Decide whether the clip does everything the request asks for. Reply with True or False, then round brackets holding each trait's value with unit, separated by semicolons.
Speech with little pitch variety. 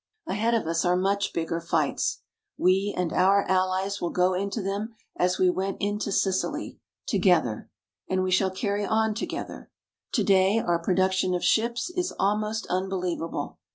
True (2.0 semitones)